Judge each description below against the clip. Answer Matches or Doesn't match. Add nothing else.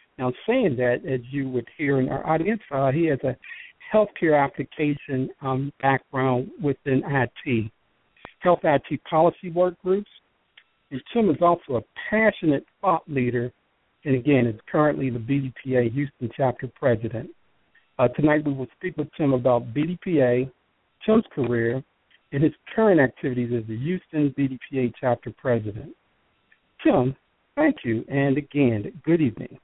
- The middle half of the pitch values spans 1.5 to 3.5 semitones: Doesn't match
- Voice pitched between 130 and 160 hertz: Matches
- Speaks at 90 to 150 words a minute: Matches